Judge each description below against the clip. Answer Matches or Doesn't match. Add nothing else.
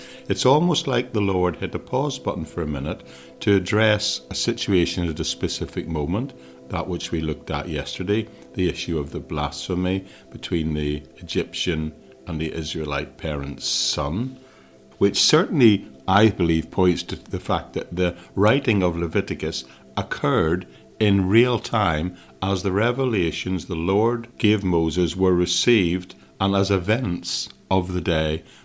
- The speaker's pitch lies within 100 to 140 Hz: Doesn't match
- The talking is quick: Doesn't match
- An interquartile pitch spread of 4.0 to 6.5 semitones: Matches